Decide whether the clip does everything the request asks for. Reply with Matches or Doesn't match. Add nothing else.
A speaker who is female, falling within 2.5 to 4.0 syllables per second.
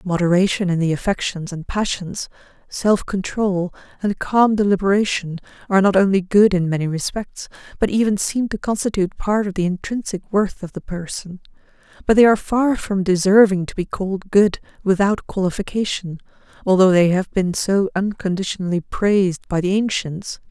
Doesn't match